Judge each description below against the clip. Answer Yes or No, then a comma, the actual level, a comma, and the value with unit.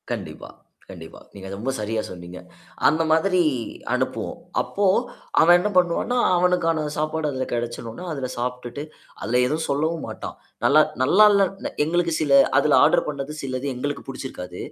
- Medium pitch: Yes, medium, 145 Hz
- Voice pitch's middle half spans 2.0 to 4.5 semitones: No, average, 4.9 semitones